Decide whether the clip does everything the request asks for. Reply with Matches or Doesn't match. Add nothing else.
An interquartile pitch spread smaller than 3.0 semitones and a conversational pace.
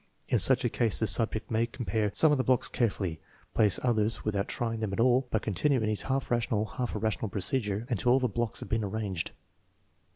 Doesn't match